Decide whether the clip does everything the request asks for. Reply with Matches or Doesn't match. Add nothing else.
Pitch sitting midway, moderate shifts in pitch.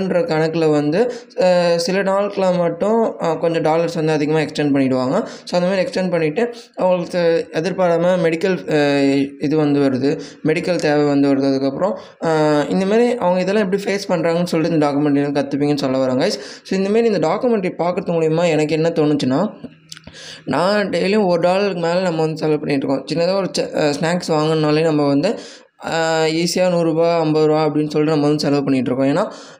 Matches